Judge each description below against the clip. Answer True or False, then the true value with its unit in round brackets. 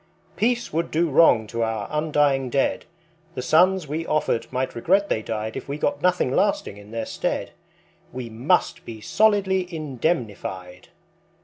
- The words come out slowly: False (150 wpm)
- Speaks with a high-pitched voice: False (140 Hz)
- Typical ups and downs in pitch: False (7.5 semitones)